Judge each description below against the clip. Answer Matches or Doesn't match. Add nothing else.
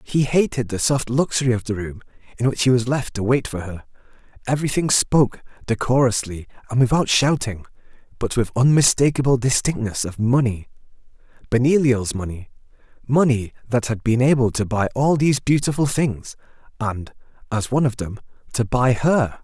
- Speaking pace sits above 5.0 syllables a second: Matches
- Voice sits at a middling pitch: Doesn't match